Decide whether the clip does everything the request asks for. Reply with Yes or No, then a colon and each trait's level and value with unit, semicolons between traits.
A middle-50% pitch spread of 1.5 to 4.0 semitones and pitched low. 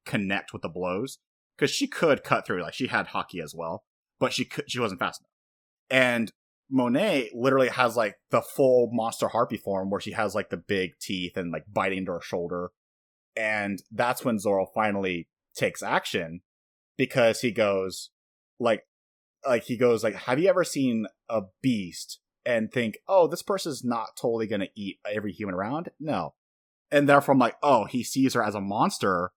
No: average, 4.6 semitones; low, 105 Hz